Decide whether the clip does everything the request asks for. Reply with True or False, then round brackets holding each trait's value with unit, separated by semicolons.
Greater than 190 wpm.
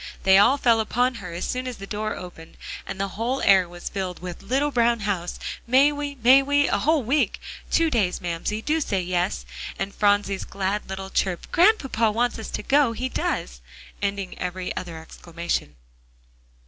False (175 wpm)